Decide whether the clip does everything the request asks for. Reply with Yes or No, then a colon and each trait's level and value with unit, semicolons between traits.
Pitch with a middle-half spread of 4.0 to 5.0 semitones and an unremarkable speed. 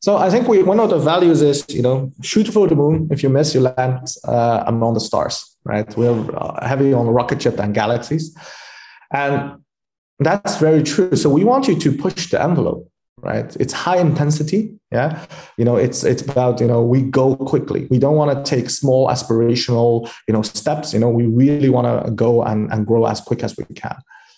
No: average, 4.3 semitones; fast, 210 wpm